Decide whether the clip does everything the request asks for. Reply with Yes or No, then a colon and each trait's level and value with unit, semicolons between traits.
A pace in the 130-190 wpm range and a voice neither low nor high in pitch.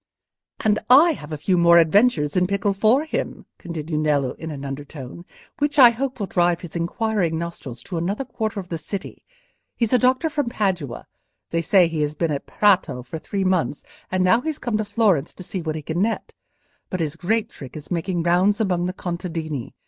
No: average, 200 wpm; medium, 180 Hz